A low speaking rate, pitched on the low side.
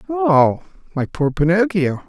No: slow, 115 wpm; medium, 180 Hz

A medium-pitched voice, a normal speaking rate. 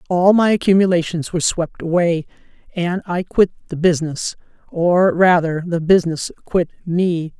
No: medium, 175 Hz; slow, 130 wpm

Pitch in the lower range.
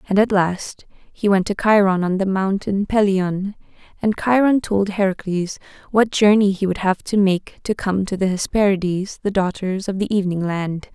No: high, 195 Hz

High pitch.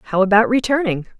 Yes: high, 220 Hz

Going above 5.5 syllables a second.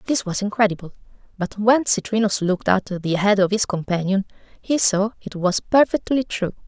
No: 5.3 syllables/s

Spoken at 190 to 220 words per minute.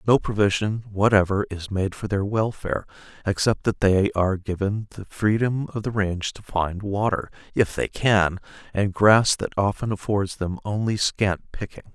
No: average, 165 wpm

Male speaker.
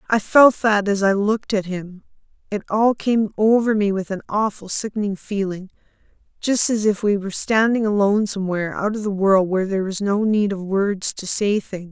No: female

